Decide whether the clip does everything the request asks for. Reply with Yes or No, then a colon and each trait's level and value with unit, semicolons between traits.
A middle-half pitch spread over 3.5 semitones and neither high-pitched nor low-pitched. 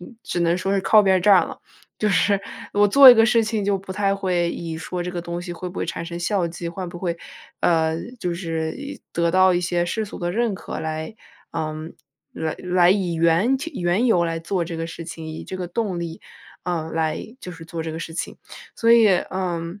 No: average, 2.9 semitones; medium, 175 Hz